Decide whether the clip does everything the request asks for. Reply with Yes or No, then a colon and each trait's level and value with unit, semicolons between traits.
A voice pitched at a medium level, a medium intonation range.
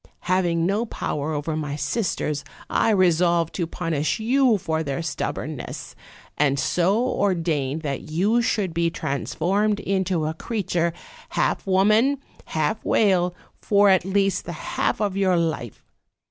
Yes: medium, 175 Hz; average, 4.1 semitones